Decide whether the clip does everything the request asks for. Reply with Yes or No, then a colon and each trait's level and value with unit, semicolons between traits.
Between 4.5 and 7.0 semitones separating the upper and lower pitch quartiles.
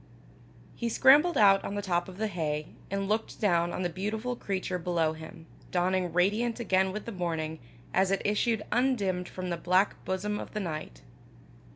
No: average, 3.3 semitones